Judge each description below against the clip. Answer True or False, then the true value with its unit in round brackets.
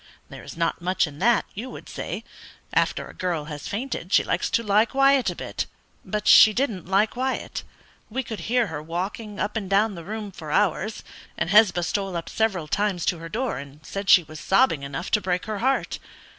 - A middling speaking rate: False (210 wpm)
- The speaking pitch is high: True (200 Hz)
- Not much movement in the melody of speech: False (4.6 semitones)